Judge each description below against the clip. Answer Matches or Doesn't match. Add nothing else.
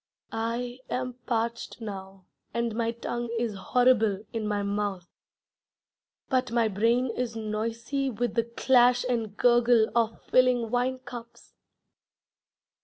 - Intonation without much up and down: Matches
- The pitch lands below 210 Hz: Doesn't match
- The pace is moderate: Doesn't match